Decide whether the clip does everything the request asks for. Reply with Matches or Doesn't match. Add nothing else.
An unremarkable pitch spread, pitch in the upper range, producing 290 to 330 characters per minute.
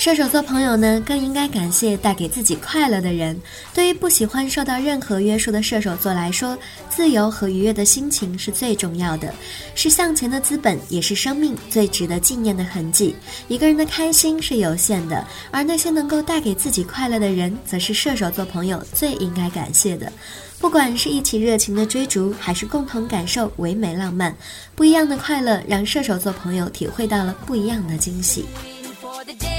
Doesn't match